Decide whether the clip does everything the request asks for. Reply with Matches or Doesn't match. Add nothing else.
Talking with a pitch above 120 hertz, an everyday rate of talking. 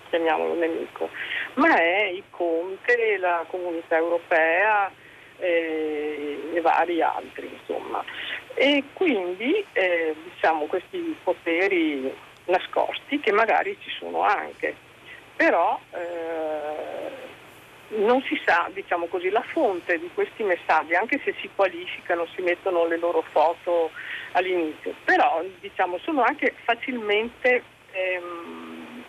Doesn't match